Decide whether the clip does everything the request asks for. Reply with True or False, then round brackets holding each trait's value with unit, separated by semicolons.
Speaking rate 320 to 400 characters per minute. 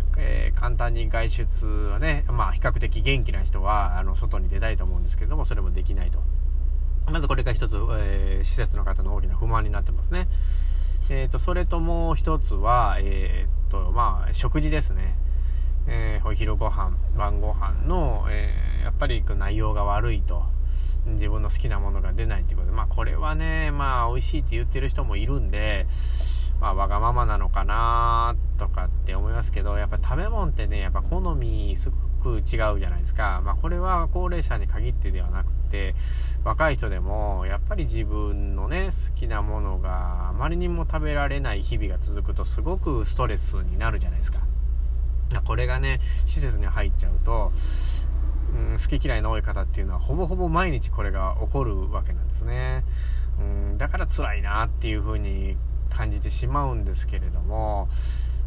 True (360 characters per minute)